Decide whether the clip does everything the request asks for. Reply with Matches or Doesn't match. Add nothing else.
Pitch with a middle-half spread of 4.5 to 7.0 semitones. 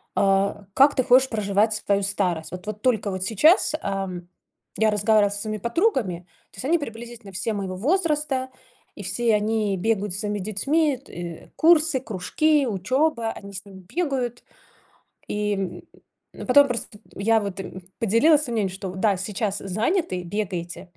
Matches